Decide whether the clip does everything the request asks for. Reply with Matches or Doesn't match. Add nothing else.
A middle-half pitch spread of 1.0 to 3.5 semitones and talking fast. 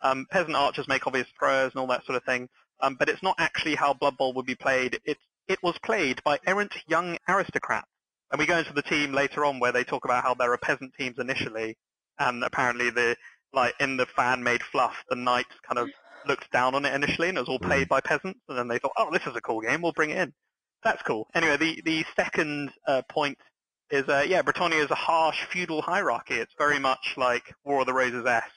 Doesn't match